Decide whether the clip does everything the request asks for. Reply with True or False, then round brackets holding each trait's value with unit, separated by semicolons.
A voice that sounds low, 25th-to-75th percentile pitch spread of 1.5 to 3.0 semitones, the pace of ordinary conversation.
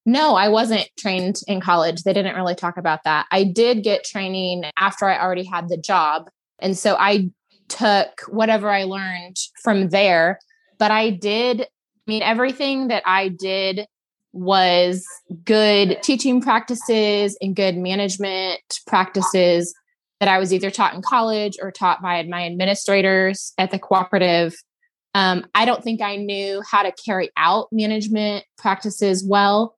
False (195 Hz; 2.5 semitones; 155 wpm)